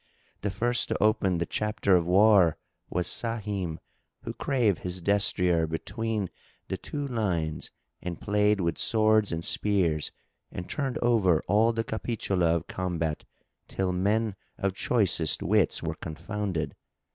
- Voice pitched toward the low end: Yes, low, 100 Hz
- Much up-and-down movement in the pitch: No, average, 3.9 semitones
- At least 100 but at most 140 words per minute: Yes, slow, 135 wpm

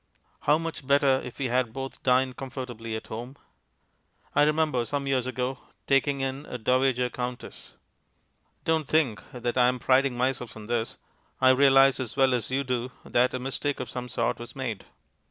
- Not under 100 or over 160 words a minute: No, average, 175 wpm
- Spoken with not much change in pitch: Yes, narrow, 1.8 semitones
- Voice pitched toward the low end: Yes, low, 130 Hz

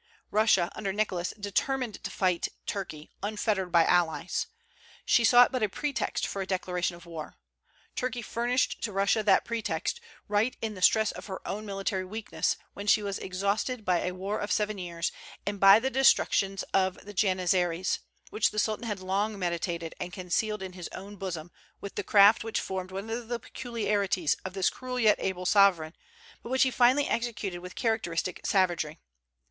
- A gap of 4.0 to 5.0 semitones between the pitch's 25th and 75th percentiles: No, average, 3.1 semitones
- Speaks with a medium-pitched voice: No, high, 200 Hz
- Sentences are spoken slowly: No, average, 175 wpm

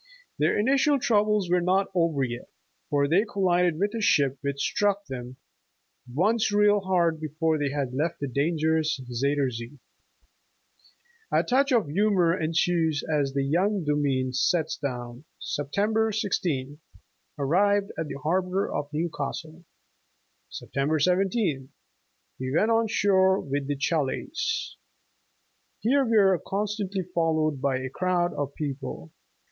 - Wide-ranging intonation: Yes, wide, 5.8 semitones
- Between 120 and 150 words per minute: Yes, average, 140 wpm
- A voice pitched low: No, medium, 165 Hz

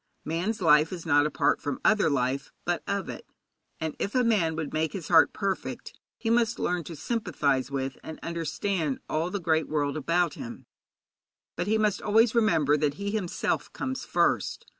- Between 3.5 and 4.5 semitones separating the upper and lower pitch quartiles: No, wide, 5.4 semitones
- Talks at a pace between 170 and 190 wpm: Yes, average, 180 wpm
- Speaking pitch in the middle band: Yes, medium, 165 Hz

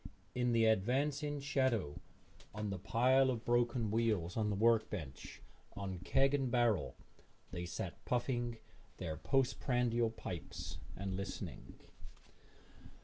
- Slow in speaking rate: Yes, slow, 125 wpm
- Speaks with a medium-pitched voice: No, low, 115 Hz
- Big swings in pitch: No, average, 4.3 semitones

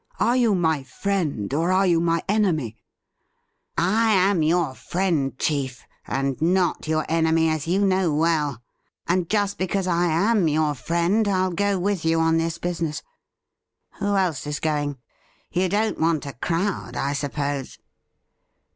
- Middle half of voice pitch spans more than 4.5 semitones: No, average, 3.8 semitones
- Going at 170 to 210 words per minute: No, average, 155 wpm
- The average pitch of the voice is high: No, medium, 165 Hz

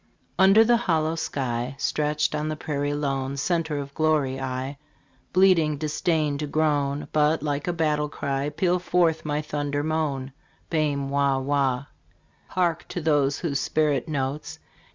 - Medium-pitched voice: Yes, medium, 150 Hz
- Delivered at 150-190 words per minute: No, average, 140 wpm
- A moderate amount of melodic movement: No, narrow, 2.2 semitones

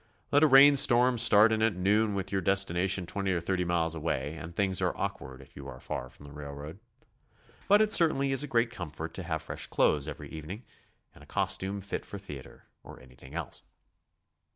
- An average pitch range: No, wide, 6.0 semitones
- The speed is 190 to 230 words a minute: Yes, fast, 205 wpm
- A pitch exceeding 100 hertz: No, very low, 95 Hz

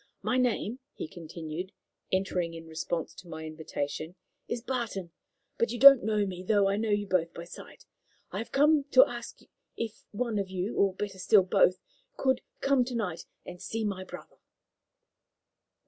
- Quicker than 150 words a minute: Yes, average, 175 wpm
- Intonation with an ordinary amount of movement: Yes, average, 4.9 semitones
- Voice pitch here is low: No, high, 200 Hz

